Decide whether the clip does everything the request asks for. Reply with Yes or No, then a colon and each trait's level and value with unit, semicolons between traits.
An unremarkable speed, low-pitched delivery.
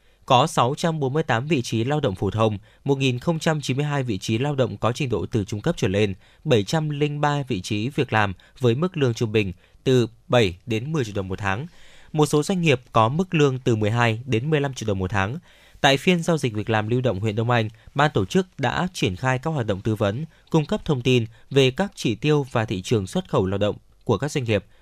Yes: average, 230 wpm; low, 125 Hz